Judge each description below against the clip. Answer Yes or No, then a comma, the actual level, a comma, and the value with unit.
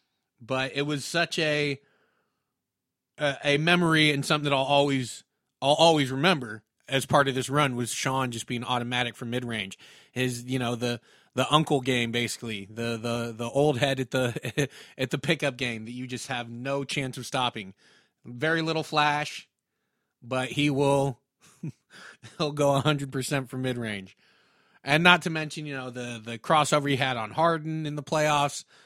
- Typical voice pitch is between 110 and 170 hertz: Yes, low, 135 Hz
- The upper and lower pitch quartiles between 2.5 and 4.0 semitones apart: Yes, average, 3.4 semitones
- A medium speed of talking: Yes, average, 170 wpm